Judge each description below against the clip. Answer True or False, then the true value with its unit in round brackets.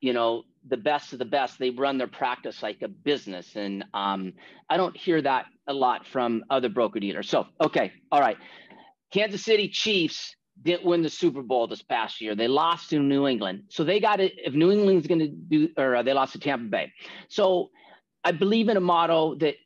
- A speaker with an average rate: False (210 wpm)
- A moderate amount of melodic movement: False (7.0 semitones)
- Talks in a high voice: False (155 Hz)